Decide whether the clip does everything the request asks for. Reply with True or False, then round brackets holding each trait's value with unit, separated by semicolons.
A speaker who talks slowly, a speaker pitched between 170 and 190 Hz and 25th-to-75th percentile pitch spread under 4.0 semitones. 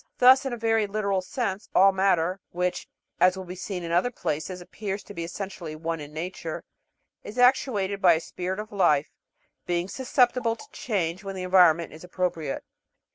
False (180 wpm; 185 Hz; 3.5 semitones)